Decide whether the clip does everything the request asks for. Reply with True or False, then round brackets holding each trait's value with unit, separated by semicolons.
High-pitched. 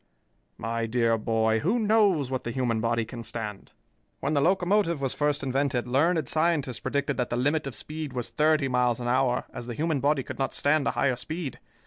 False (135 Hz)